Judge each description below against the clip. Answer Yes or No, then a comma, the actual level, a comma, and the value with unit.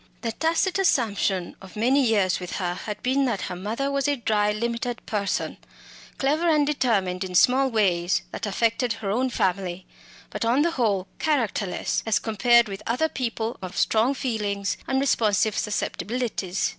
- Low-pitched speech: No, high, 225 Hz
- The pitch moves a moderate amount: Yes, average, 4.6 semitones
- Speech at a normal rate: Yes, average, 160 wpm